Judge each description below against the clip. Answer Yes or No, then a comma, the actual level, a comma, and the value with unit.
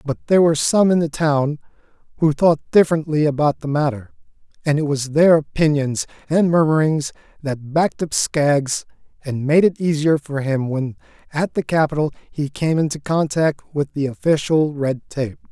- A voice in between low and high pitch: Yes, medium, 150 Hz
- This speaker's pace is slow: No, average, 165 wpm